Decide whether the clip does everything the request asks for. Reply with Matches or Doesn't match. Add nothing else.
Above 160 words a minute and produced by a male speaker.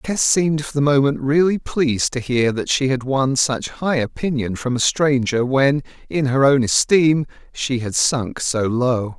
Matches